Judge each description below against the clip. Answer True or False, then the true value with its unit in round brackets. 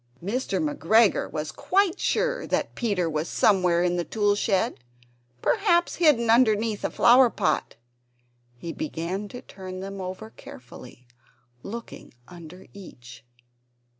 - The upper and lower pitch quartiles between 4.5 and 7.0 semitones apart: True (5.2 semitones)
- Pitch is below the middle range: False (200 Hz)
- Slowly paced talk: True (125 wpm)